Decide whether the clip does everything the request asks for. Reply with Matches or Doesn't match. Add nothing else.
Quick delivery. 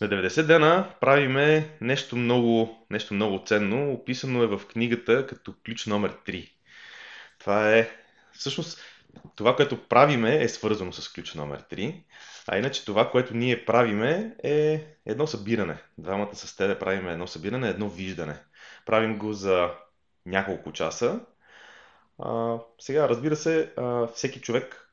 Doesn't match